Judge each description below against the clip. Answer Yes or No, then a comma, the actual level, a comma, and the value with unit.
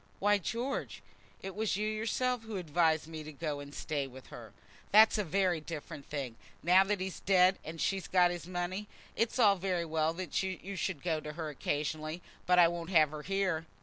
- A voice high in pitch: No, medium, 175 Hz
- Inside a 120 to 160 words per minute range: No, average, 200 wpm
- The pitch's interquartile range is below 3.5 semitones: No, average, 3.9 semitones